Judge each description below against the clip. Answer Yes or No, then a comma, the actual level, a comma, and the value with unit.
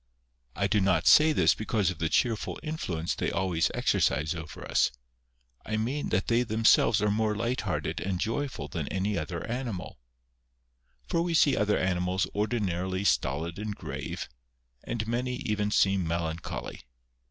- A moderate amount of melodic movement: Yes, average, 4.4 semitones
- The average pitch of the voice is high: No, low, 105 Hz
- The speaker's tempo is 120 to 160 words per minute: Yes, average, 155 wpm